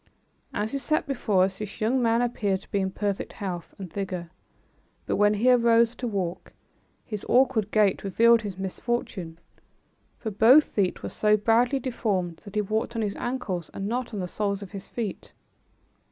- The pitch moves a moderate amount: Yes, average, 3.4 semitones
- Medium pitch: No, high, 210 Hz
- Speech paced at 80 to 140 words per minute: No, average, 180 wpm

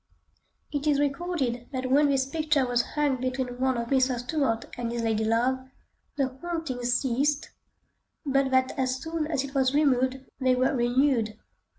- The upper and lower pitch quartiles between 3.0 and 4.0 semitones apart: No, narrow, 2.5 semitones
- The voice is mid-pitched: No, very high, 260 Hz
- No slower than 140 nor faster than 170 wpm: Yes, average, 165 wpm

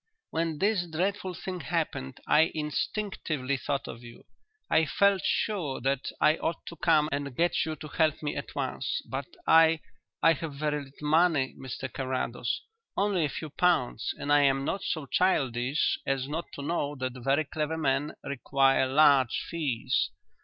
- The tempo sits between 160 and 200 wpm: Yes, average, 165 wpm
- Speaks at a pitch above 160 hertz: No, medium, 150 Hz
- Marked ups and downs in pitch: No, average, 3.3 semitones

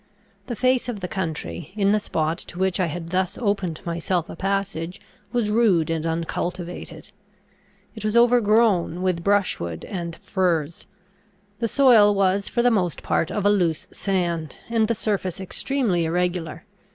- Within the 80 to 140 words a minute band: No, average, 155 wpm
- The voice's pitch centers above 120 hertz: Yes, medium, 185 Hz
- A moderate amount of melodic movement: Yes, average, 3.8 semitones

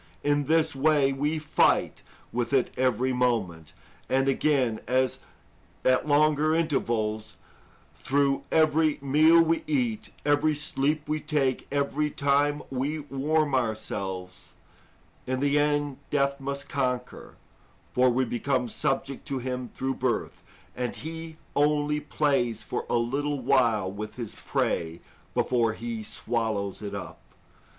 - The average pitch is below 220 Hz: Yes, low, 135 Hz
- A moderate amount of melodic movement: Yes, average, 3.6 semitones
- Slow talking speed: Yes, slow, 125 wpm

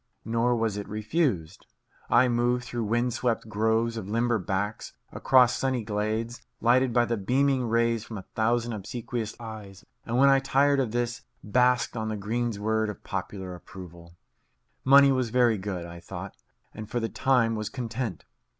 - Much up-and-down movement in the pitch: No, average, 2.7 semitones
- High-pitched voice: No, low, 115 Hz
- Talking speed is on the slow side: No, average, 165 wpm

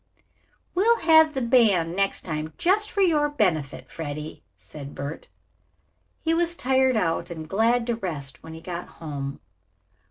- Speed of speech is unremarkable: Yes, average, 150 wpm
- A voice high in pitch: Yes, high, 195 Hz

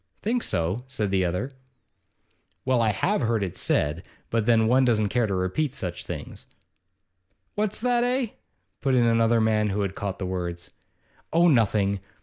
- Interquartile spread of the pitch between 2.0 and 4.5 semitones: No, average, 5.1 semitones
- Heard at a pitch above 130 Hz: No, low, 110 Hz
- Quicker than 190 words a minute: No, average, 165 wpm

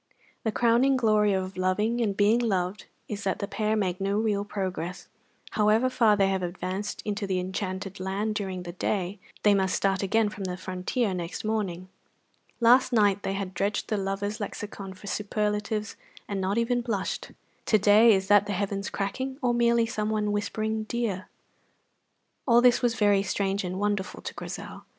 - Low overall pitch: No, high, 205 Hz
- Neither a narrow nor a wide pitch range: No, narrow, 2.2 semitones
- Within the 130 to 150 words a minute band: No, average, 175 wpm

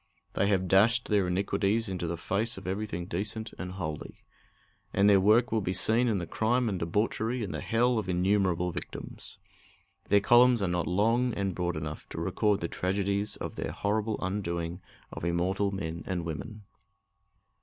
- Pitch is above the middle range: No, low, 100 Hz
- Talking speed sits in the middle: Yes, average, 175 wpm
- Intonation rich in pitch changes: No, average, 3.4 semitones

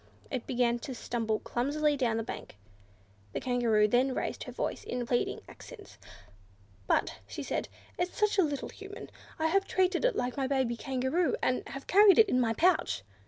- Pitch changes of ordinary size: No, wide, 6.9 semitones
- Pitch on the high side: Yes, very high, 265 Hz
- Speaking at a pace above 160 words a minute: Yes, average, 180 wpm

